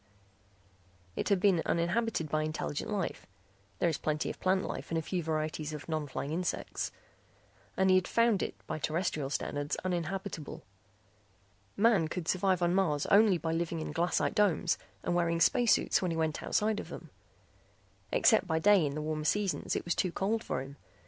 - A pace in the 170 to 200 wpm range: Yes, average, 180 wpm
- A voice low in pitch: No, medium, 170 Hz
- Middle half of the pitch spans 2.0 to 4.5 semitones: Yes, average, 3.6 semitones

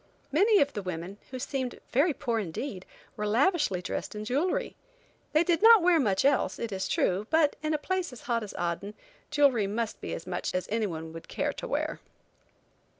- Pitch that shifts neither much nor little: No, wide, 7.6 semitones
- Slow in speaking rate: No, average, 195 wpm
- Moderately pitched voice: No, high, 240 Hz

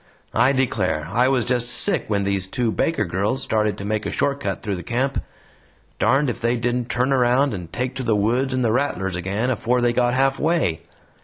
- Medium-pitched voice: No, low, 120 Hz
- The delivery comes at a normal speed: No, fast, 210 wpm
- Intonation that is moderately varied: Yes, average, 4.1 semitones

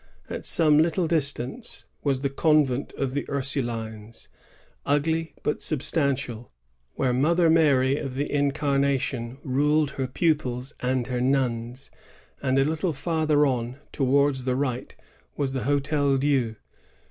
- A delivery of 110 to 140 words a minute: Yes, slow, 135 wpm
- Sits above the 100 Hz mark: Yes, medium, 140 Hz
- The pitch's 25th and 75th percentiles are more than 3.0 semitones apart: No, narrow, 2.6 semitones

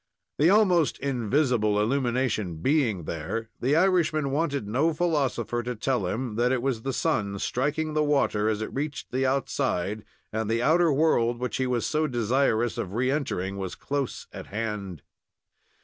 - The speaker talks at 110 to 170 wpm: Yes, average, 165 wpm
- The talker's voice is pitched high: No, low, 125 Hz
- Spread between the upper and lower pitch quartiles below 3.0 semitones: No, average, 5.1 semitones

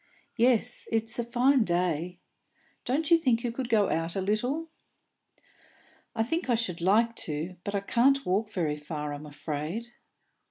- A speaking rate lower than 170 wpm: Yes, average, 160 wpm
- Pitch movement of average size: No, wide, 5.9 semitones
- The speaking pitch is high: Yes, high, 220 Hz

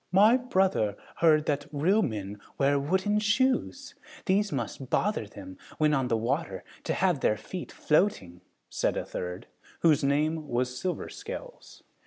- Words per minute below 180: Yes, average, 150 wpm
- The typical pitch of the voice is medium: Yes, medium, 155 Hz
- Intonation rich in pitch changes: Yes, wide, 7.9 semitones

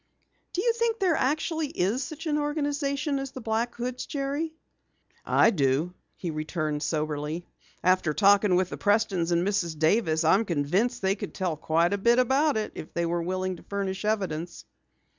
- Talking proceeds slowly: No, average, 175 wpm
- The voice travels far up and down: Yes, wide, 8.2 semitones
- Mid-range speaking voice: No, high, 200 Hz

